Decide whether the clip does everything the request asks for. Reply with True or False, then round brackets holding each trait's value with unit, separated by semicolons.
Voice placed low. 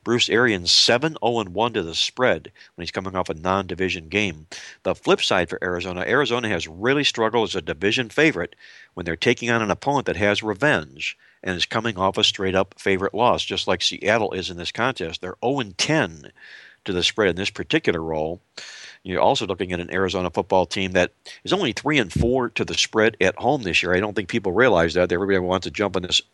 True (95 Hz)